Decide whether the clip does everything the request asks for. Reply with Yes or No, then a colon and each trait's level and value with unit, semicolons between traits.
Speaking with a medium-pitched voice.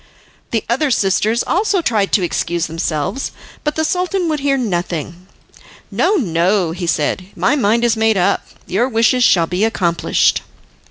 No: high, 220 Hz